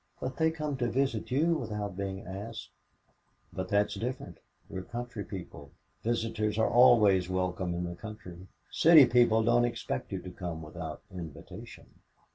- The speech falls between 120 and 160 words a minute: Yes, average, 155 wpm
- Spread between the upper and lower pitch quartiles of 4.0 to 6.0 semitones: Yes, average, 4.7 semitones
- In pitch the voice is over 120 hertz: No, low, 105 Hz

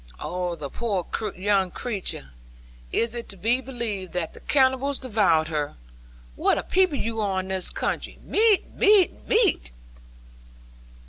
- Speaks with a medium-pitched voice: No, high, 215 Hz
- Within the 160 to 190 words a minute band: No, average, 140 wpm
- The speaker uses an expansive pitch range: Yes, wide, 6.2 semitones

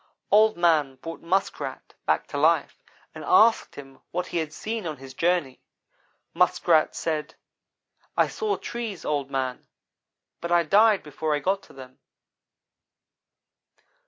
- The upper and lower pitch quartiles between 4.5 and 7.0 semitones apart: Yes, average, 5.1 semitones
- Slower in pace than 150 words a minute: Yes, slow, 135 wpm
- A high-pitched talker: No, medium, 165 Hz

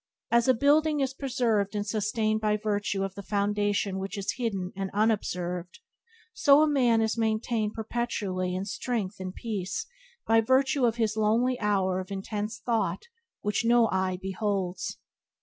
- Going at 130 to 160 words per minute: Yes, average, 155 wpm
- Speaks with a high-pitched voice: Yes, high, 215 Hz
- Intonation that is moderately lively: Yes, average, 3.3 semitones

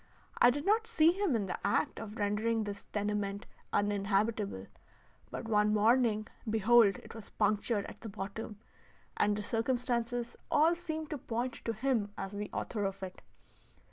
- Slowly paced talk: No, average, 160 wpm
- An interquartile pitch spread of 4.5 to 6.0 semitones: No, average, 2.9 semitones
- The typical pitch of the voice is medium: No, high, 220 Hz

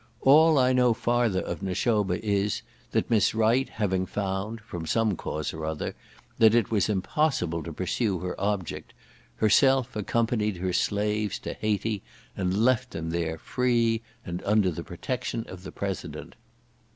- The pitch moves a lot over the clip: No, average, 4.0 semitones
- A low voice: Yes, low, 105 Hz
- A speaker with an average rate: Yes, average, 150 wpm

